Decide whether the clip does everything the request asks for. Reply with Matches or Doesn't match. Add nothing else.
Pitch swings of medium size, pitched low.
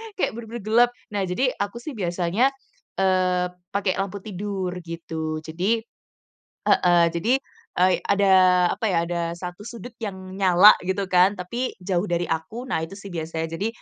Doesn't match